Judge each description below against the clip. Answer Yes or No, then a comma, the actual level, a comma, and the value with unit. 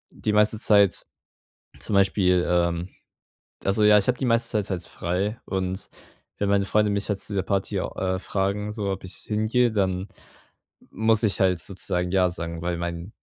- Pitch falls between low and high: No, low, 100 Hz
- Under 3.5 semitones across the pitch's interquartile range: Yes, narrow, 2.5 semitones